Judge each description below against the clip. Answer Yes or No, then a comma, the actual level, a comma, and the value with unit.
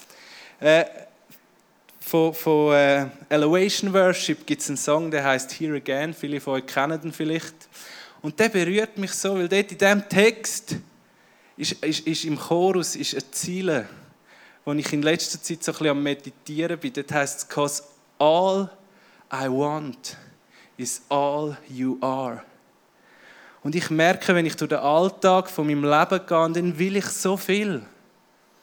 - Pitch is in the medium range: Yes, medium, 155 Hz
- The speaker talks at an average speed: Yes, average, 155 wpm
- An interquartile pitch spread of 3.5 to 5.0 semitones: Yes, average, 4.1 semitones